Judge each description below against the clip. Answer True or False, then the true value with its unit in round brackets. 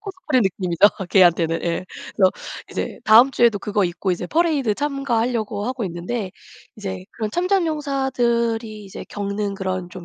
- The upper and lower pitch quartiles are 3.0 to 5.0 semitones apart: False (5.4 semitones)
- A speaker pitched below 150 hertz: False (215 Hz)